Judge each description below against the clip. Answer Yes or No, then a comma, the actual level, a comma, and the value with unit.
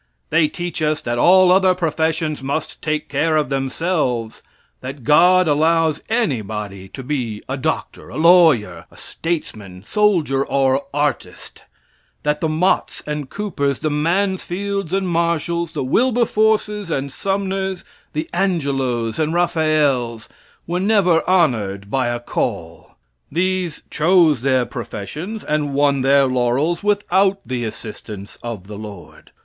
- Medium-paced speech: No, slow, 130 wpm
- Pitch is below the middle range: No, medium, 155 Hz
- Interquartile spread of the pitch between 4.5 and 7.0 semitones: Yes, wide, 5.6 semitones